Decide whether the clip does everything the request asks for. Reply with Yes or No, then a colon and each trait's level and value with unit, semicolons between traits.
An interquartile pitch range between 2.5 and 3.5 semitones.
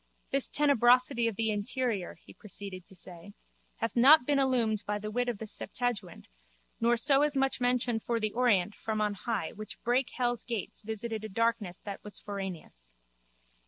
Yes: average, 3.2 semitones